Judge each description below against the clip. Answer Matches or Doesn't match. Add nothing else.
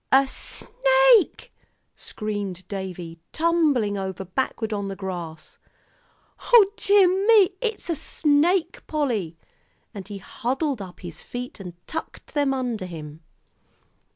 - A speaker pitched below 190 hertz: Doesn't match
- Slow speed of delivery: Matches